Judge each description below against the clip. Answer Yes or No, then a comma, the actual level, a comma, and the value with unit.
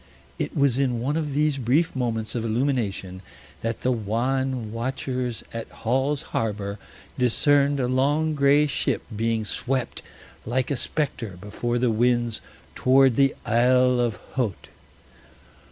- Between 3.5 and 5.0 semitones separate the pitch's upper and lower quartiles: No, average, 3.0 semitones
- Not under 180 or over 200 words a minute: No, slow, 135 wpm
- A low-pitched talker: Yes, low, 125 Hz